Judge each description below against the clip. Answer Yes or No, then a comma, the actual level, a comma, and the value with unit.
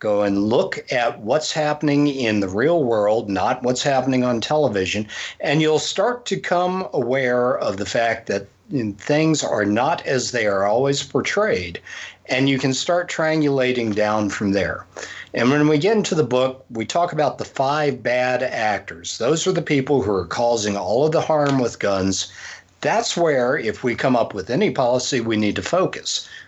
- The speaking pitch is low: Yes, low, 130 Hz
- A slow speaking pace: No, average, 185 wpm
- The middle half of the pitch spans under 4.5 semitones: No, average, 5.2 semitones